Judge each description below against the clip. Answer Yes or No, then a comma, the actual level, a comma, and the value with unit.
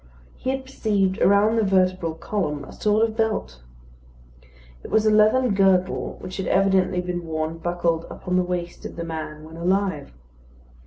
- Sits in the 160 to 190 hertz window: Yes, medium, 185 Hz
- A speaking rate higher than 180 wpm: No, average, 165 wpm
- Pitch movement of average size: Yes, average, 3.8 semitones